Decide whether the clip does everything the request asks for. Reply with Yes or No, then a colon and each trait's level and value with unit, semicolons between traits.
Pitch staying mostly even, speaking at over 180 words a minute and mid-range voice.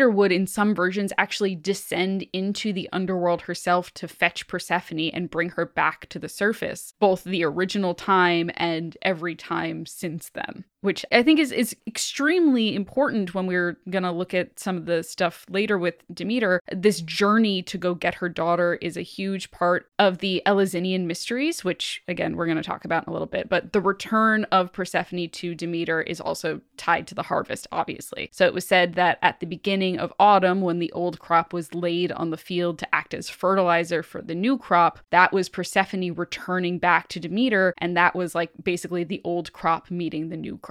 Yes: narrow, 2.2 semitones; average, 195 wpm; medium, 180 Hz